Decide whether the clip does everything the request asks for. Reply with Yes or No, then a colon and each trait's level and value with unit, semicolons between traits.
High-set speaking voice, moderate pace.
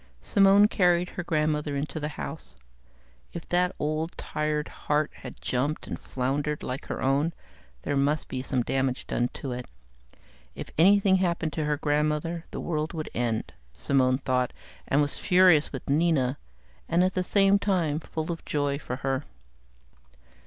No: medium, 150 Hz; average, 160 wpm